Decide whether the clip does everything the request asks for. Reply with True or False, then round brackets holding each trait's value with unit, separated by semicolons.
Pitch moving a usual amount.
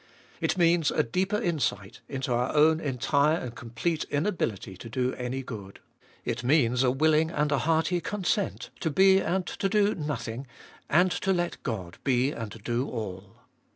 False (6.1 semitones)